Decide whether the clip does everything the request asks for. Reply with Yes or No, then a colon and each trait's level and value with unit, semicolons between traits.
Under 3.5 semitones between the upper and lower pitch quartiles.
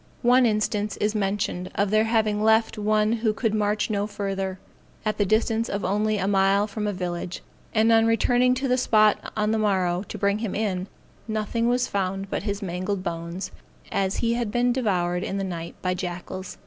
Yes: narrow, 2.5 semitones